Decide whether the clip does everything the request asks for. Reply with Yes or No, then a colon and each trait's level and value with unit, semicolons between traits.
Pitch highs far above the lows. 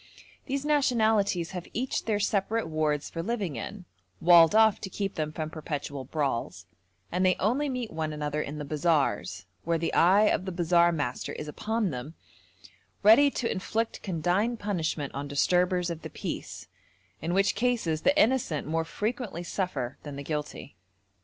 Yes: wide, 5.7 semitones